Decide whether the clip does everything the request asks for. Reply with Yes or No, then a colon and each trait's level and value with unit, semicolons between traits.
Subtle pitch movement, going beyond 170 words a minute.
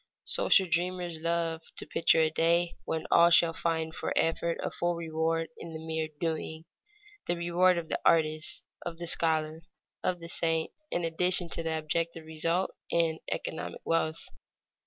No: narrow, 1.1 semitones; average, 160 wpm